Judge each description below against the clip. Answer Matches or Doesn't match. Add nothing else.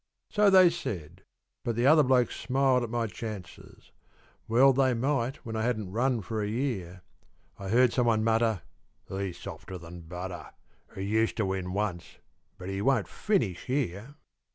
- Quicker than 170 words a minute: Doesn't match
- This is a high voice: Doesn't match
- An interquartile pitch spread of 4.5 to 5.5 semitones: Matches